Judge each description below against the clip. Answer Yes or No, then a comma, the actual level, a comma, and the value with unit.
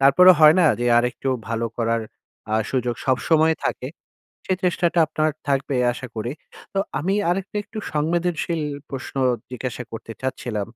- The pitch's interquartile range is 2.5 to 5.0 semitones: No, wide, 5.6 semitones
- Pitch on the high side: No, medium, 140 Hz